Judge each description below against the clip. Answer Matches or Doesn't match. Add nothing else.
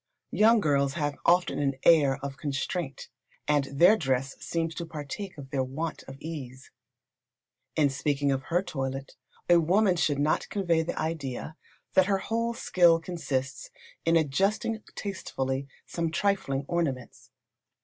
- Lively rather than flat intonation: Doesn't match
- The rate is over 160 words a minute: Doesn't match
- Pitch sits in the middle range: Matches